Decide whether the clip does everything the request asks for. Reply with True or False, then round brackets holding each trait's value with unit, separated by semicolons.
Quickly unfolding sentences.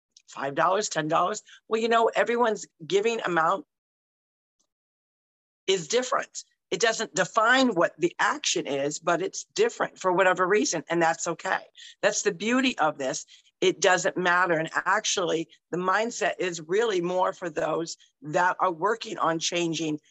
False (145 wpm)